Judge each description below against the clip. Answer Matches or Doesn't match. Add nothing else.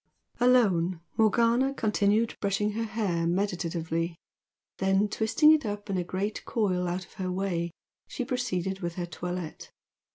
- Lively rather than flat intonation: Doesn't match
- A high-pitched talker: Matches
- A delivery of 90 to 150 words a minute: Matches